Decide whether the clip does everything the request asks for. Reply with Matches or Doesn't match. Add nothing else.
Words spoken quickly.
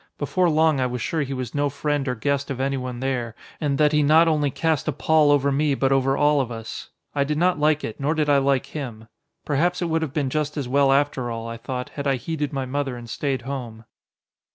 Matches